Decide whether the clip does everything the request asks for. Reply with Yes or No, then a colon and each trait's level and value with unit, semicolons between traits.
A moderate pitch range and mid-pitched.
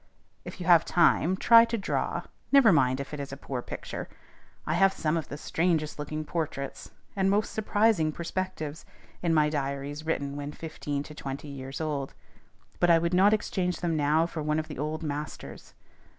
Yes: average, 3.6 semitones; medium, 155 Hz